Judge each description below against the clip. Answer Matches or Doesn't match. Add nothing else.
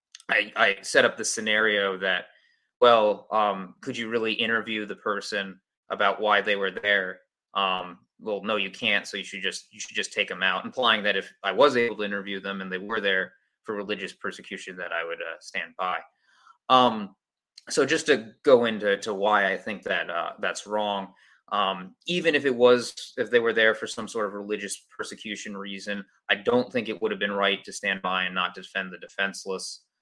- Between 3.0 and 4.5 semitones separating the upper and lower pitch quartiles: Doesn't match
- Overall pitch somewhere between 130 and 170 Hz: Doesn't match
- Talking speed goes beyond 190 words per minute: Matches